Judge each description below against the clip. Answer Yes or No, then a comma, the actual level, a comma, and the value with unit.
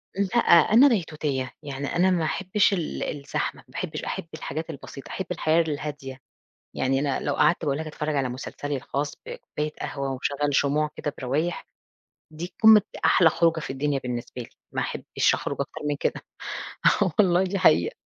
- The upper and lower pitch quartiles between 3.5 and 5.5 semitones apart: Yes, average, 3.9 semitones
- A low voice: No, medium, 150 Hz